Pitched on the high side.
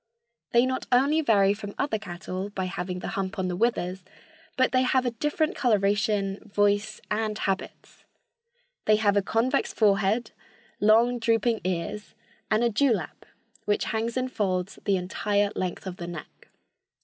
Yes: high, 210 Hz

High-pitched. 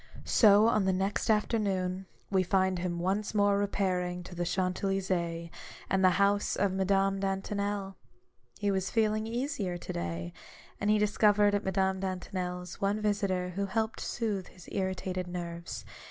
Yes: high, 195 Hz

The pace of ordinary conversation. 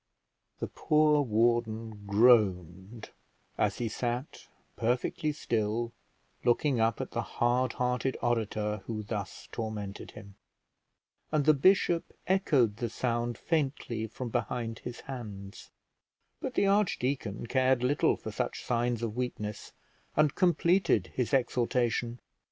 No: slow, 120 wpm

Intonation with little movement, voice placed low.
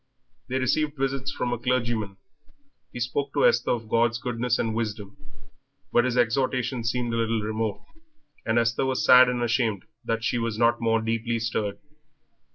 Yes: narrow, 1.8 semitones; low, 115 Hz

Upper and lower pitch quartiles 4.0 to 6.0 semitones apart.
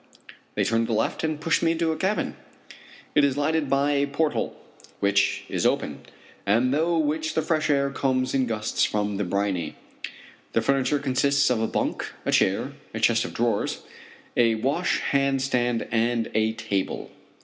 Yes: average, 4.6 semitones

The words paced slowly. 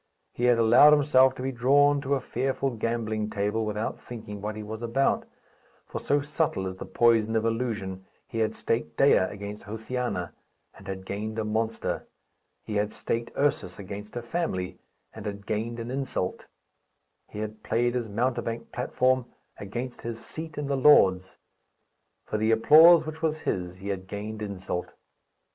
No: average, 165 wpm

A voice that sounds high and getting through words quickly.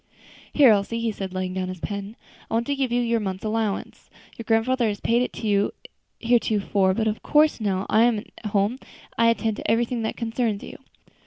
Yes: high, 220 Hz; fast, 215 wpm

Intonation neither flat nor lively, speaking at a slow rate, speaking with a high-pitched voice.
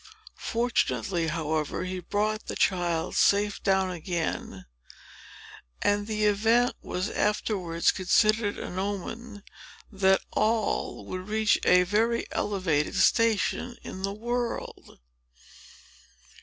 Yes: average, 3.0 semitones; slow, 100 wpm; high, 200 Hz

